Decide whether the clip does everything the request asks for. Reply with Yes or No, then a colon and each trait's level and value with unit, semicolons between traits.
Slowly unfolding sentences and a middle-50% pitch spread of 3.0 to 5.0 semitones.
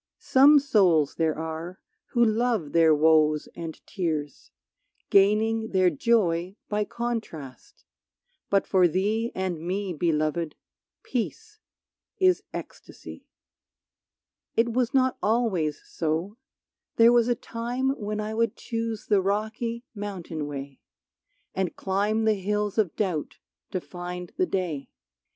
No: slow, 120 wpm; wide, 5.4 semitones